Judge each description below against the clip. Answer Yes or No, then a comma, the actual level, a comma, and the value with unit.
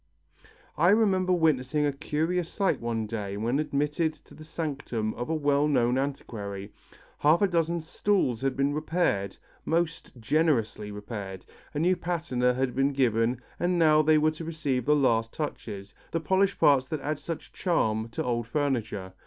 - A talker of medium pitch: Yes, medium, 145 Hz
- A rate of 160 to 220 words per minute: Yes, average, 165 wpm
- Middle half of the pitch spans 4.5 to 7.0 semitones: Yes, wide, 5.6 semitones